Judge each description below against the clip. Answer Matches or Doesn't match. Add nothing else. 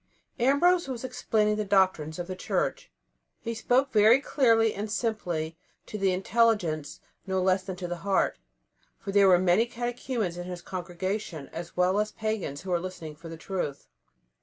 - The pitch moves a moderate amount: Matches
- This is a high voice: Matches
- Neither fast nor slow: Matches